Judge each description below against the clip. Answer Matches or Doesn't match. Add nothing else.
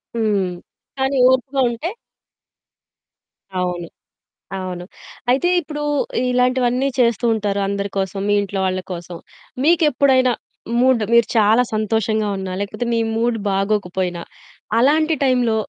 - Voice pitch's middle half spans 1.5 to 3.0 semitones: Doesn't match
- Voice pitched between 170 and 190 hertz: Doesn't match